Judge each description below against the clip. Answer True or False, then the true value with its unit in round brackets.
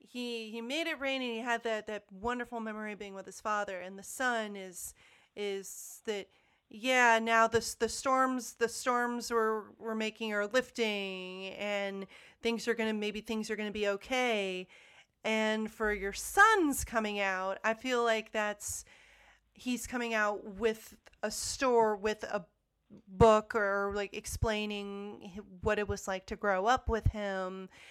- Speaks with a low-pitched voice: False (215 Hz)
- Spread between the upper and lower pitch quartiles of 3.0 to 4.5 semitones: False (2.4 semitones)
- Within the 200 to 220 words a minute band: False (165 wpm)